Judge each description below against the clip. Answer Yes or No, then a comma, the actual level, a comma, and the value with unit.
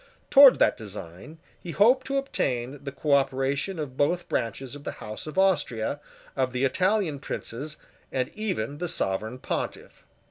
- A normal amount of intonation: No, wide, 5.9 semitones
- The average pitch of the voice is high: No, medium, 140 Hz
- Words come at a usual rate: Yes, average, 155 wpm